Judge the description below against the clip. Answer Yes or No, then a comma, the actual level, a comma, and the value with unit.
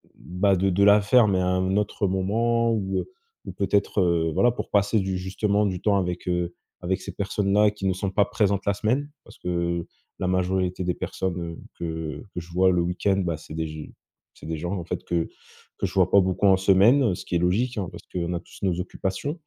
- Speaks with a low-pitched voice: Yes, very low, 95 Hz